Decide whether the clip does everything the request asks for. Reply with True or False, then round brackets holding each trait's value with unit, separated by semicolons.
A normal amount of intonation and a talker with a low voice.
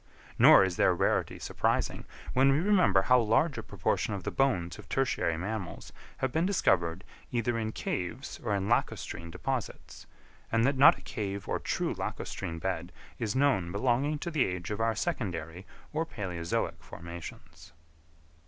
False (7.1 semitones; 110 Hz)